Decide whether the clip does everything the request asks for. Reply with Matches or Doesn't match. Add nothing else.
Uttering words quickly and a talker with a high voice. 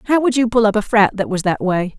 Matches